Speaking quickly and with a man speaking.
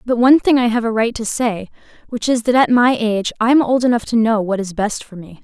No: fast, 285 wpm; female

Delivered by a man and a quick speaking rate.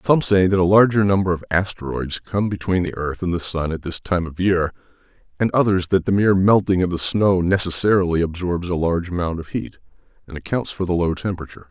Yes: male; fast, 215 wpm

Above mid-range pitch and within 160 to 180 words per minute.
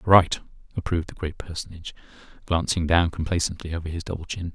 No: very low, 85 Hz; average, 170 wpm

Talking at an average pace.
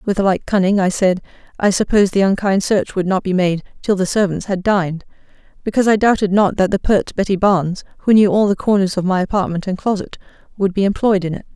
No: fast, 225 wpm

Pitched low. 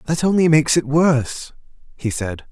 No: medium, 145 Hz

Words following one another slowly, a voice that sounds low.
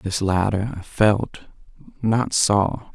Yes: slow, 100 wpm; low, 105 Hz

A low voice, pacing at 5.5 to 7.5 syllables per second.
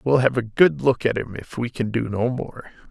No: low, 120 Hz; 4.9 syllables/s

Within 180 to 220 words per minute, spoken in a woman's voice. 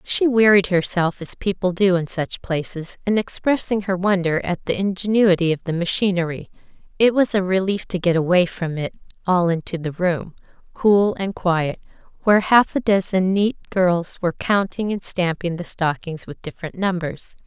No: average, 170 wpm; female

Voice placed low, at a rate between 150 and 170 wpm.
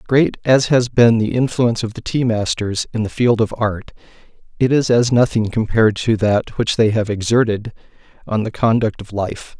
No: low, 115 Hz; average, 195 wpm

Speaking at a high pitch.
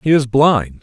No: low, 130 Hz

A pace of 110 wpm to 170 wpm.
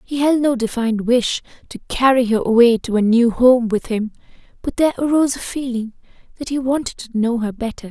No: fast, 205 wpm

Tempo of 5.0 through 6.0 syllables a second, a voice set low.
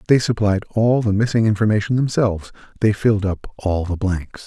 Yes: 5.5 syllables/s; low, 105 Hz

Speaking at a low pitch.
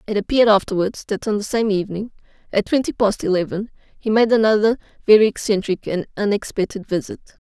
No: high, 210 Hz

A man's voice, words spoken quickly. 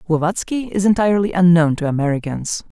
No: male; slow, 130 wpm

